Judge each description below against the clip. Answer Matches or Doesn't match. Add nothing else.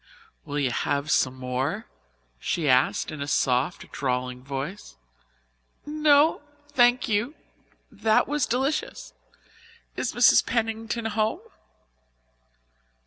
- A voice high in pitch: Matches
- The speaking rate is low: Matches